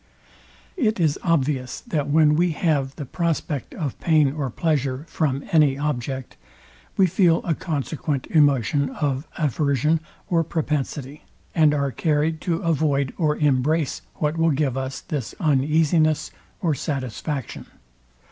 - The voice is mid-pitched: Yes, medium, 150 Hz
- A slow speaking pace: Yes, slow, 130 wpm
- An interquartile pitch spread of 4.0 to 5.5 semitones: No, average, 2.7 semitones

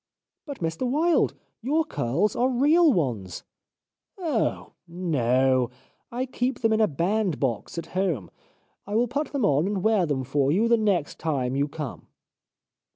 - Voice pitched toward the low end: No, high, 190 Hz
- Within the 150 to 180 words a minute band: Yes, average, 165 wpm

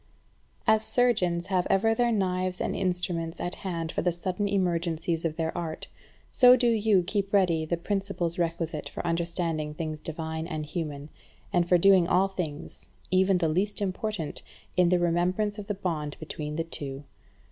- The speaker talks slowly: No, average, 170 wpm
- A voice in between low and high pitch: Yes, medium, 175 Hz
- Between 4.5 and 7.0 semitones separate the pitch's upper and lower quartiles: No, average, 3.0 semitones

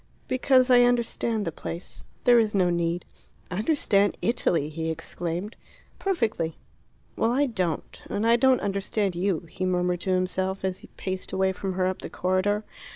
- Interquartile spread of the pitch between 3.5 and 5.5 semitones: Yes, average, 4.2 semitones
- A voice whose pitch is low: No, high, 190 Hz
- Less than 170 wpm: Yes, average, 160 wpm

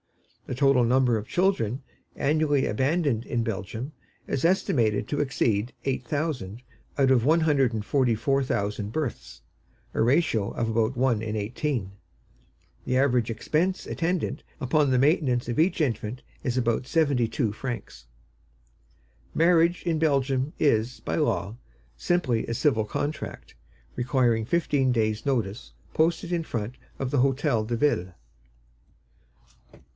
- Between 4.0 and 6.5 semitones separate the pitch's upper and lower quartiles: Yes, average, 4.6 semitones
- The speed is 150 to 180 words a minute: No, slow, 135 wpm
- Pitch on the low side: Yes, low, 130 Hz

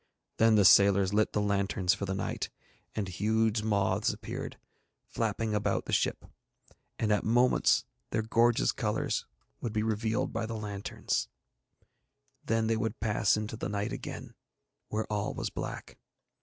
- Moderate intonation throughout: No, narrow, 1.7 semitones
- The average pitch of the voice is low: Yes, low, 105 Hz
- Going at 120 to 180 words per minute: Yes, average, 150 wpm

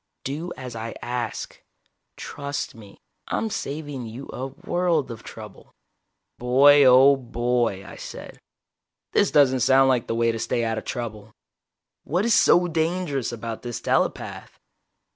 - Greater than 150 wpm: No, average, 145 wpm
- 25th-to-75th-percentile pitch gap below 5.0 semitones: Yes, average, 3.8 semitones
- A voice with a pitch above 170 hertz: No, low, 130 Hz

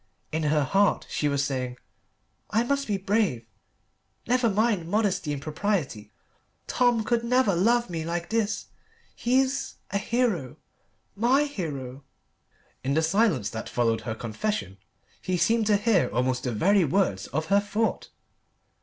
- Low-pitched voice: No, high, 195 Hz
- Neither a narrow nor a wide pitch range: No, wide, 8.3 semitones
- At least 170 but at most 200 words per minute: No, average, 145 wpm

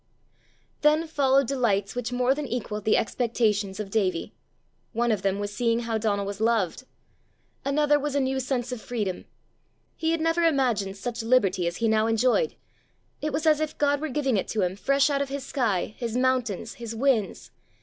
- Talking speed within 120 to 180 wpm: No, average, 190 wpm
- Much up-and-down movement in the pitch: No, average, 4.8 semitones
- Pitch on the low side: No, high, 240 Hz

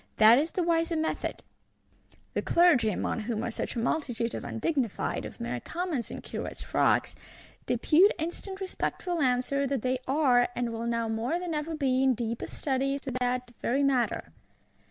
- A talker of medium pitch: No, very high, 265 Hz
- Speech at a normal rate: Yes, average, 175 wpm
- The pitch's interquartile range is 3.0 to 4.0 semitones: No, average, 5.2 semitones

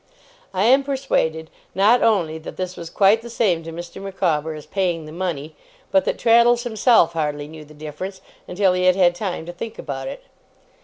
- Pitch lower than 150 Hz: No, medium, 180 Hz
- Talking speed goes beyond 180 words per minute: Yes, average, 195 wpm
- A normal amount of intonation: Yes, average, 4.3 semitones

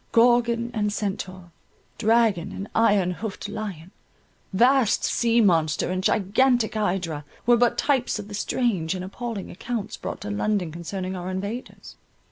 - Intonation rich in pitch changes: No, average, 4.0 semitones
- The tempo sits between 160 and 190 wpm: No, average, 140 wpm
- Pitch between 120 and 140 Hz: No, high, 205 Hz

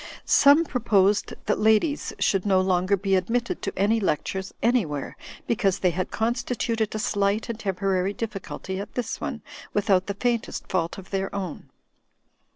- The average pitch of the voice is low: No, high, 200 Hz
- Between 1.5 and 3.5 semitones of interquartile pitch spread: Yes, average, 3.1 semitones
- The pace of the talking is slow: No, average, 155 wpm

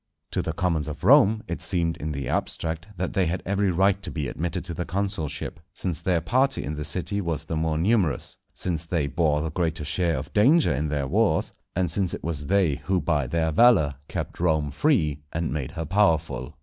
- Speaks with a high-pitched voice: No, very low, 85 Hz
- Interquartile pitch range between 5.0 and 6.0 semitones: No, average, 3.6 semitones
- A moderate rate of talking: No, fast, 210 wpm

